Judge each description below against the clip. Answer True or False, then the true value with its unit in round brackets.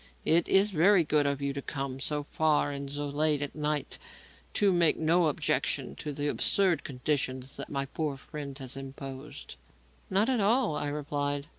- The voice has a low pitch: False (145 Hz)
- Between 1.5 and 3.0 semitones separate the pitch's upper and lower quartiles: True (2.4 semitones)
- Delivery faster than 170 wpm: True (180 wpm)